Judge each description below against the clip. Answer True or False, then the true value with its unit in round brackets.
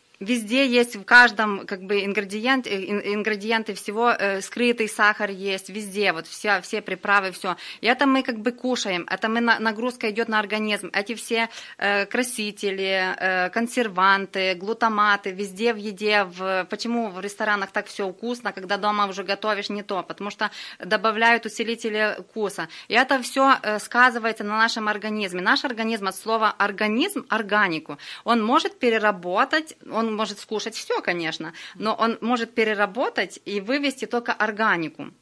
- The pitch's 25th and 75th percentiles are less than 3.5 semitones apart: True (2.5 semitones)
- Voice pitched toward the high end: True (215 Hz)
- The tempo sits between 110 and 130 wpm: False (155 wpm)